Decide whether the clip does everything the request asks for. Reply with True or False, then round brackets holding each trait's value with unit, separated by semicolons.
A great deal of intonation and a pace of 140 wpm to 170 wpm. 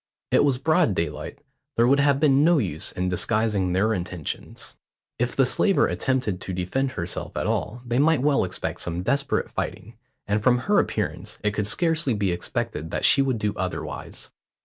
False (6.9 semitones; 180 wpm)